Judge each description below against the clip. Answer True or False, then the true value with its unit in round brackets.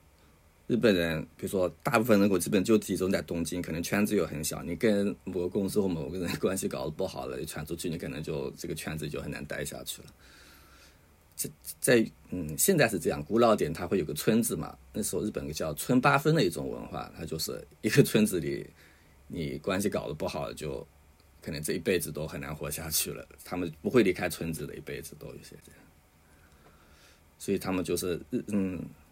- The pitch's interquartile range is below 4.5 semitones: True (2.9 semitones)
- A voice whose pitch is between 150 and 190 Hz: False (80 Hz)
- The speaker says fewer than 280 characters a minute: False (300 characters per minute)